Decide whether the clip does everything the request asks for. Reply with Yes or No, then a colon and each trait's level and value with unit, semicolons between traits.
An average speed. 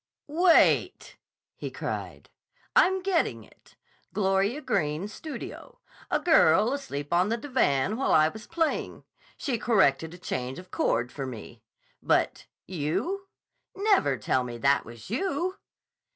No: slow, 125 wpm